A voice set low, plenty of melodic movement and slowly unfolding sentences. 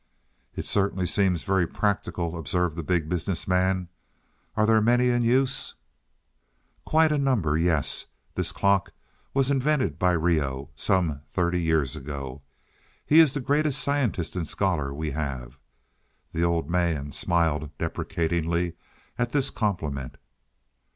Yes: very low, 90 Hz; wide, 6.2 semitones; slow, 130 wpm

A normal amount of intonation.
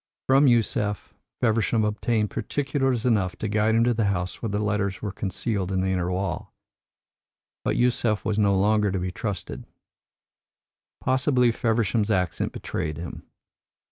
Yes: average, 3.3 semitones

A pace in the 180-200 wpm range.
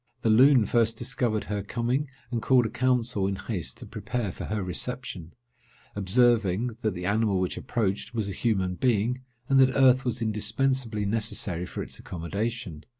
No: average, 165 wpm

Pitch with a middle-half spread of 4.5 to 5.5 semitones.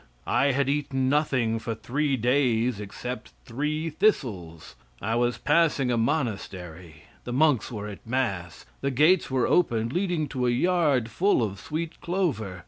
Yes: average, 5.1 semitones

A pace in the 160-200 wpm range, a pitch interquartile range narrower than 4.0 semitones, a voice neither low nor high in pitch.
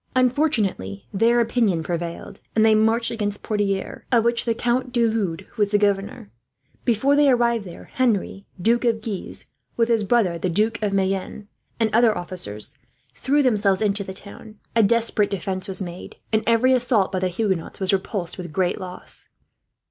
No: average, 170 wpm; average, 3.6 semitones; high, 210 Hz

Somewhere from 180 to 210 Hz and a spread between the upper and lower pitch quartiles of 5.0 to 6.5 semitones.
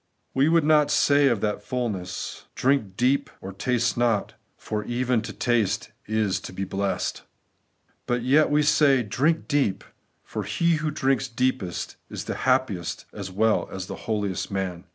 No: low, 120 Hz; average, 5.3 semitones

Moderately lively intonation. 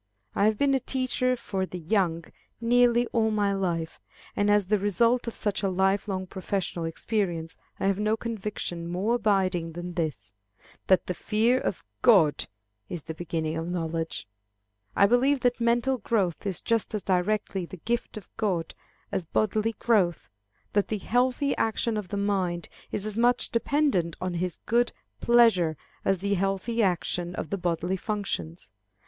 Yes: average, 4.5 semitones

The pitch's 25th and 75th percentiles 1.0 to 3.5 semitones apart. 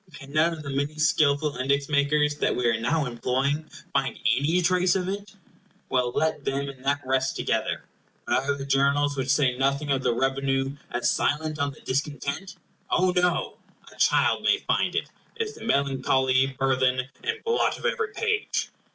Yes: average, 2.8 semitones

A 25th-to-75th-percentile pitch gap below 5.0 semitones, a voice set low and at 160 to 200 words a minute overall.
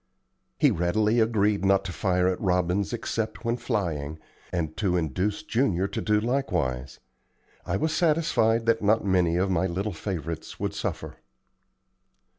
No: average, 4.2 semitones; very low, 95 Hz; average, 145 wpm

